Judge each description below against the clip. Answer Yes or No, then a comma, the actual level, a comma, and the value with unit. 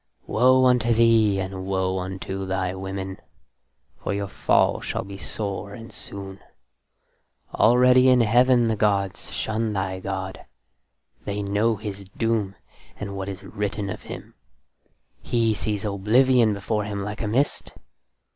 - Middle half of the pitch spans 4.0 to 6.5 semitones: No, average, 2.8 semitones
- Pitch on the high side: No, low, 100 Hz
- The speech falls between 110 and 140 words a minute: Yes, slow, 135 wpm